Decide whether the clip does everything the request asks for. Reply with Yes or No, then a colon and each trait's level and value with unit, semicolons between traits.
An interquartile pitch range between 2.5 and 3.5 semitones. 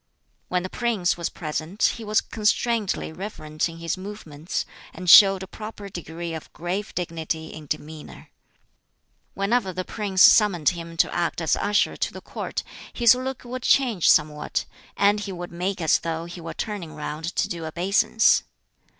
No: average, 4.1 semitones